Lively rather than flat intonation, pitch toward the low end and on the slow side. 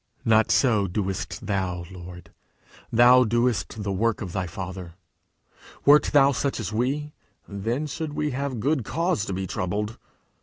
No: wide, 5.9 semitones; low, 110 Hz; average, 150 wpm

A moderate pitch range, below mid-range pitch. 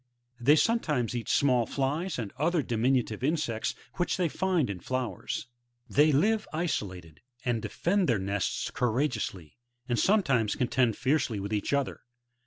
No: wide, 5.8 semitones; low, 130 Hz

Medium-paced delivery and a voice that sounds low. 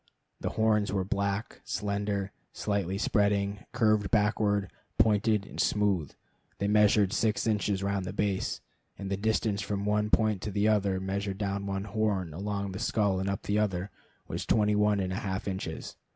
Yes: average, 170 wpm; low, 100 Hz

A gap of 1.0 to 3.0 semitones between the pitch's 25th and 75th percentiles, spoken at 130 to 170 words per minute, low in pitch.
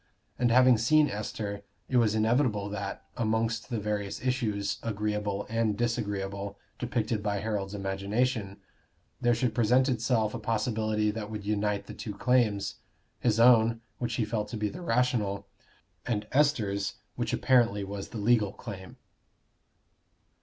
Yes: average, 2.7 semitones; average, 140 wpm; low, 110 Hz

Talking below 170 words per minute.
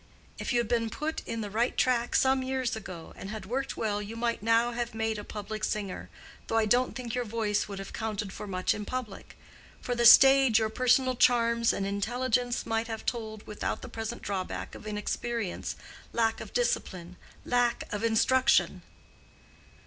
No: average, 180 wpm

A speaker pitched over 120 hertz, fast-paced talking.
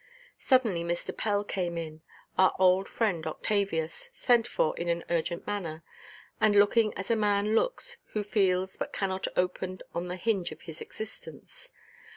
No: high, 190 Hz; average, 160 wpm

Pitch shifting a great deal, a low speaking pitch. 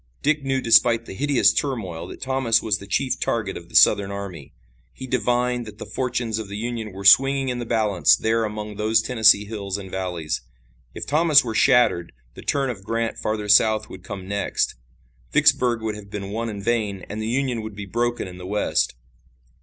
No: average, 3.4 semitones; low, 110 Hz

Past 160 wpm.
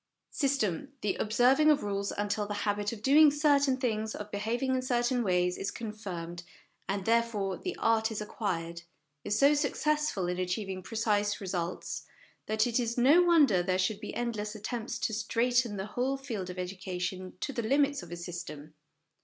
Yes: average, 170 wpm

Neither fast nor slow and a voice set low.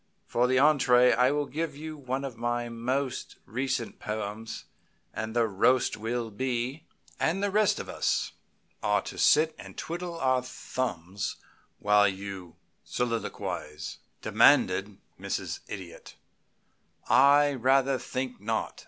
No: slow, 130 wpm; low, 125 Hz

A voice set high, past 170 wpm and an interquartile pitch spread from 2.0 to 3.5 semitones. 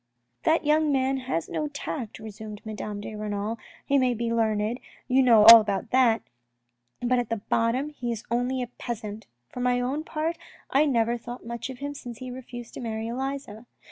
Yes: high, 240 Hz; average, 190 wpm; average, 3.1 semitones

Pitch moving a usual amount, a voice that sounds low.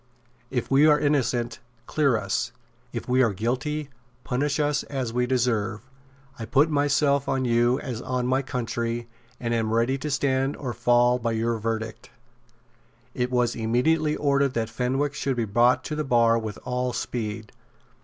Yes: average, 3.0 semitones; low, 125 Hz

